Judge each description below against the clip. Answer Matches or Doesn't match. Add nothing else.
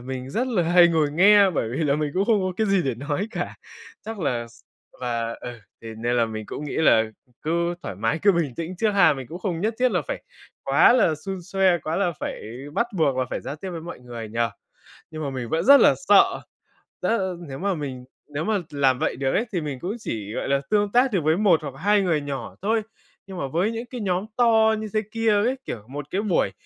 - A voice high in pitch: Doesn't match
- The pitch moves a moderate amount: Doesn't match